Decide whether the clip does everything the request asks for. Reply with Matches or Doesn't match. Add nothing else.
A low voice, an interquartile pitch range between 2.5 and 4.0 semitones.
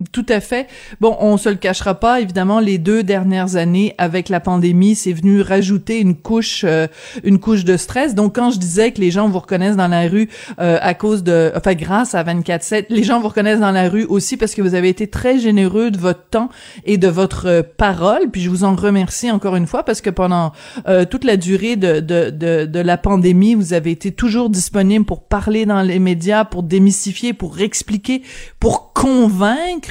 Doesn't match